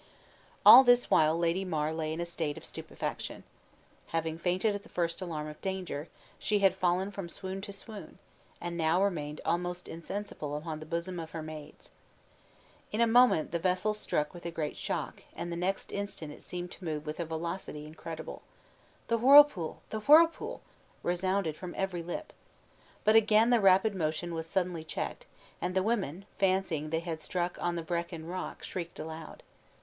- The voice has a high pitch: No, medium, 175 Hz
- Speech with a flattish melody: No, average, 3.2 semitones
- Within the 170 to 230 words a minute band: Yes, average, 175 wpm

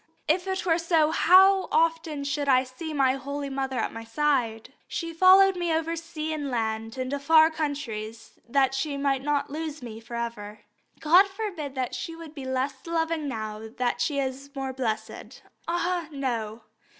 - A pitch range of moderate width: Yes, average, 4.3 semitones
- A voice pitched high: Yes, very high, 280 Hz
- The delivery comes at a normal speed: Yes, average, 175 wpm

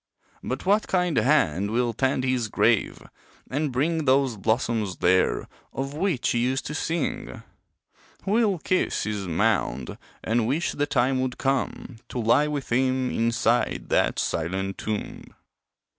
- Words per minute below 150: Yes, average, 140 wpm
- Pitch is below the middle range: Yes, low, 130 Hz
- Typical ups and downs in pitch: Yes, average, 4.5 semitones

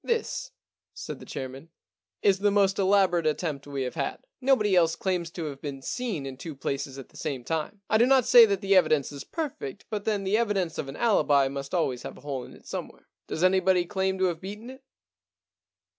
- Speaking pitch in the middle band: Yes, medium, 175 Hz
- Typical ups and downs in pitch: No, wide, 6.3 semitones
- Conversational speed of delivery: No, fast, 220 wpm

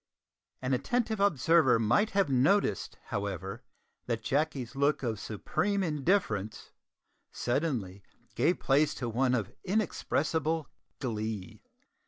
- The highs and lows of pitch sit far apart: Yes, wide, 6.8 semitones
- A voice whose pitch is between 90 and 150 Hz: Yes, low, 135 Hz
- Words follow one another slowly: Yes, slow, 105 wpm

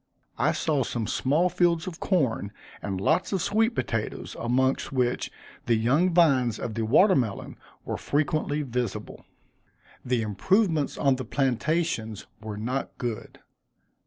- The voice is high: No, low, 130 Hz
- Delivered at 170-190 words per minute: No, slow, 135 wpm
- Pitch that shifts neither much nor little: No, wide, 6.2 semitones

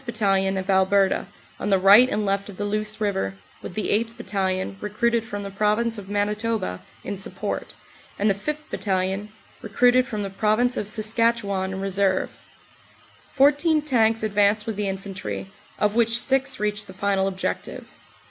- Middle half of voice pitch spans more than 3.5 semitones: No, average, 2.7 semitones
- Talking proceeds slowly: No, average, 165 wpm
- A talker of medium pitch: No, high, 205 Hz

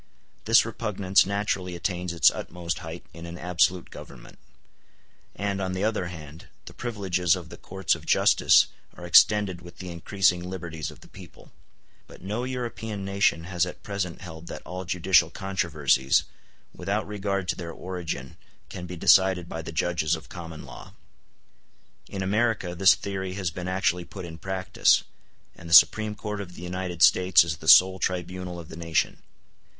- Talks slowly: No, average, 165 wpm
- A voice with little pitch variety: Yes, narrow, 2.3 semitones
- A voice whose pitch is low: Yes, very low, 90 Hz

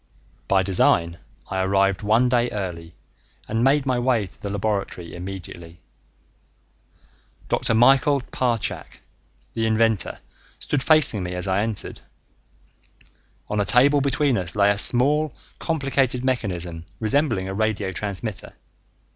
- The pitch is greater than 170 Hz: No, low, 110 Hz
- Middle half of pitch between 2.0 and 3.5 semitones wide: No, average, 5.1 semitones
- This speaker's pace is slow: Yes, slow, 125 wpm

